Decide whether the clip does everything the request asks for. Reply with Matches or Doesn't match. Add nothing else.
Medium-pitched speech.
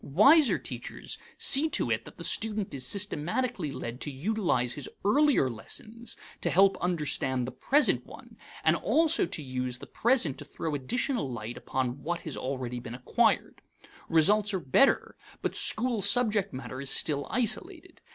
Matches